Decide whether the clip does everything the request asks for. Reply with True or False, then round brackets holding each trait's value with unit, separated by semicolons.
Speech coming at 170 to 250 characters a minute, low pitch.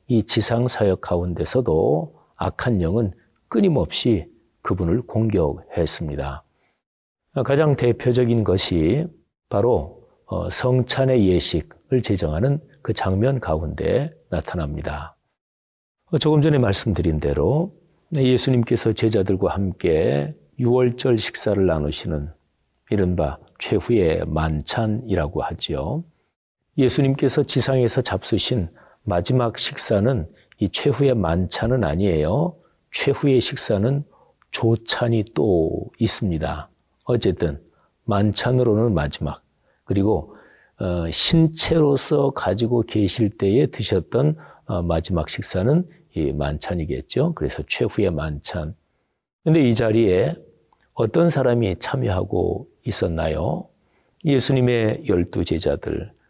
True (235 characters per minute; 110 Hz)